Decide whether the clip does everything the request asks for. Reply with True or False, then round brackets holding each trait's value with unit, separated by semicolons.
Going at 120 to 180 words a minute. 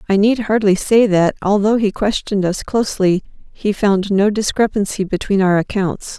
True (165 wpm)